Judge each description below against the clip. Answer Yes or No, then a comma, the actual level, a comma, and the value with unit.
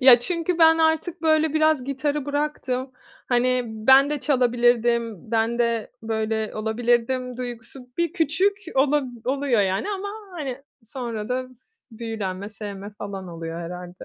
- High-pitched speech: Yes, very high, 250 Hz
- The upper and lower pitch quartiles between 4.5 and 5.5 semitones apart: Yes, average, 5.0 semitones